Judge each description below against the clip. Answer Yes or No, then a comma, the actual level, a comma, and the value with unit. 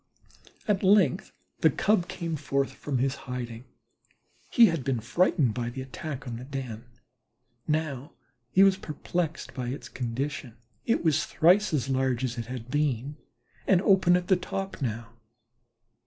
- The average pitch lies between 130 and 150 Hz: Yes, medium, 140 Hz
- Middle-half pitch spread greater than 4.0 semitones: Yes, wide, 5.6 semitones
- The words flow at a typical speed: Yes, average, 155 wpm